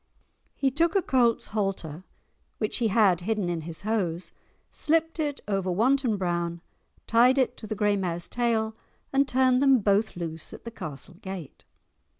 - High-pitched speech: Yes, high, 215 Hz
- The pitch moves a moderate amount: No, wide, 6.2 semitones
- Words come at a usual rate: Yes, average, 160 wpm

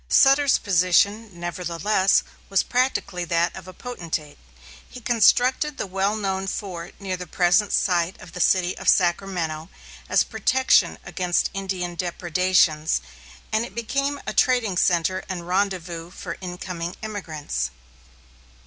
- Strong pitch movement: No, average, 3.2 semitones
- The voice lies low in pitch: No, medium, 185 Hz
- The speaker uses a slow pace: Yes, slow, 130 wpm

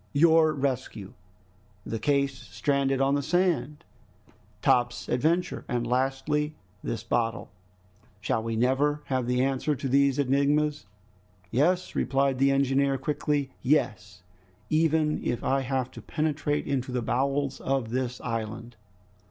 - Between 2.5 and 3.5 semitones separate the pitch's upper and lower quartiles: Yes, average, 3.0 semitones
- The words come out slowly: Yes, slow, 125 wpm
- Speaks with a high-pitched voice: No, low, 135 Hz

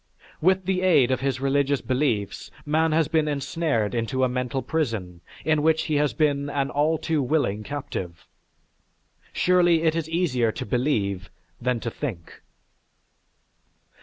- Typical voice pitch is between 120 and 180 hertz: Yes, medium, 140 Hz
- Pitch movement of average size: Yes, average, 4.5 semitones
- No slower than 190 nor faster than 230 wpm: No, average, 145 wpm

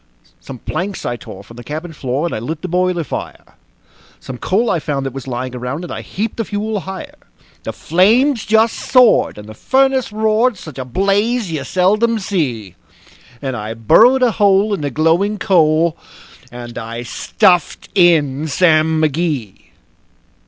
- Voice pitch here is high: No, medium, 170 Hz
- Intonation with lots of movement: Yes, wide, 7.6 semitones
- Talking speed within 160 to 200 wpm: Yes, average, 165 wpm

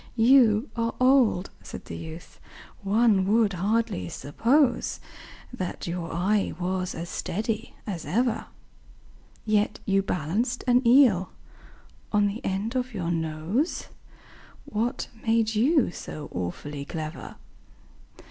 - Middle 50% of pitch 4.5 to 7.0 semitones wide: Yes, average, 5.1 semitones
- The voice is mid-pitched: No, high, 205 Hz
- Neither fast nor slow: No, slow, 115 wpm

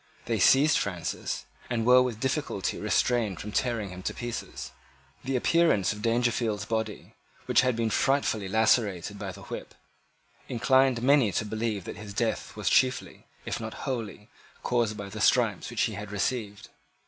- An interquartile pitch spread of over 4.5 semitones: No, average, 3.2 semitones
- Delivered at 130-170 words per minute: Yes, average, 160 wpm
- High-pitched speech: No, low, 115 Hz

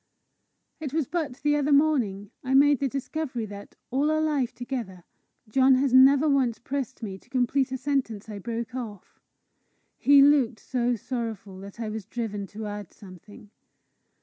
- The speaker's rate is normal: Yes, average, 165 wpm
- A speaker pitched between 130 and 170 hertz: No, very high, 250 Hz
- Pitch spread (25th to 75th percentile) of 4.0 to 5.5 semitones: Yes, average, 4.6 semitones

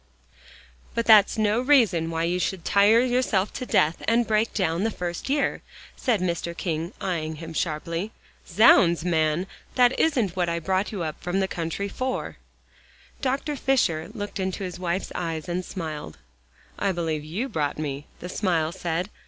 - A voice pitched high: No, medium, 180 Hz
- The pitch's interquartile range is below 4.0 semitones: No, average, 4.6 semitones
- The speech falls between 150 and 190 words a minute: Yes, average, 165 wpm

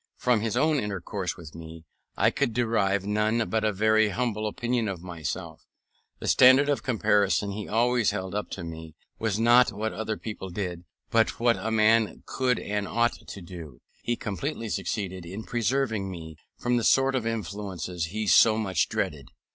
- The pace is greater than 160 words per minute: Yes, average, 180 wpm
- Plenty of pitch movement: No, average, 3.6 semitones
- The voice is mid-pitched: No, low, 105 Hz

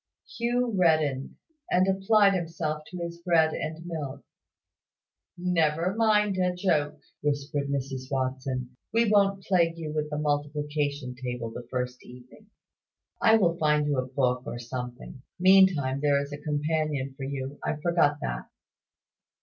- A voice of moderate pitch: Yes, medium, 150 Hz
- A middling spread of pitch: Yes, average, 4.7 semitones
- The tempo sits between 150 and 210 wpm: No, average, 140 wpm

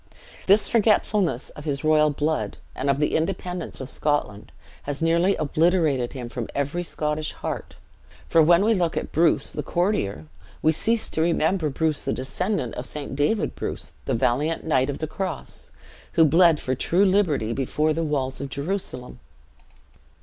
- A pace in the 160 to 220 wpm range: Yes, average, 165 wpm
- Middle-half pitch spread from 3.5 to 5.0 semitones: Yes, average, 4.1 semitones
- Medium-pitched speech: Yes, medium, 155 Hz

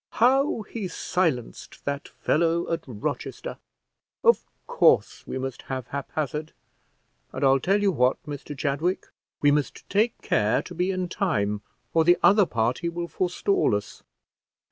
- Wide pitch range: Yes, wide, 5.7 semitones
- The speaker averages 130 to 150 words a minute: Yes, average, 145 wpm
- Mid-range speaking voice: Yes, medium, 160 Hz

